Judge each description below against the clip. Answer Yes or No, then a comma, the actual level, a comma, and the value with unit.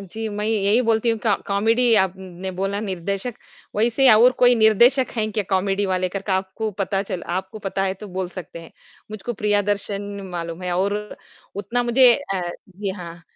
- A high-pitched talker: Yes, high, 200 Hz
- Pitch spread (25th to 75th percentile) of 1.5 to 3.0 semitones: Yes, average, 2.7 semitones